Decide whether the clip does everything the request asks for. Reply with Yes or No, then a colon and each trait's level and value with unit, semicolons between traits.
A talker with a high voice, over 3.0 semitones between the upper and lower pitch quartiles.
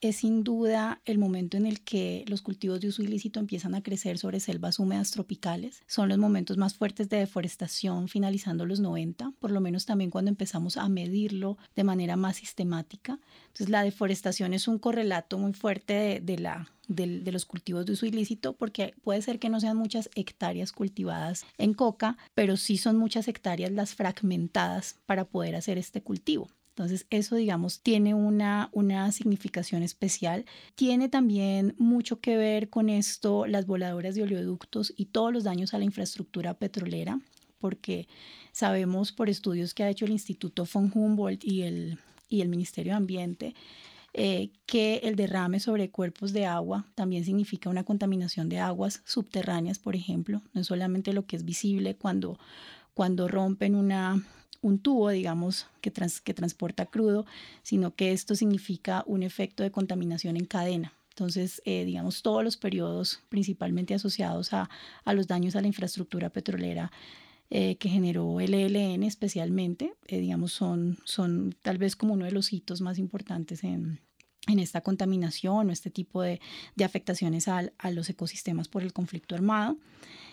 No: high, 195 Hz; narrow, 2.5 semitones